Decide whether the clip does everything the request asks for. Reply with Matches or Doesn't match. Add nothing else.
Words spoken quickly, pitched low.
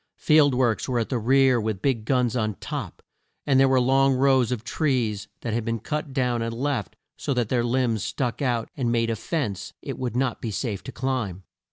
Matches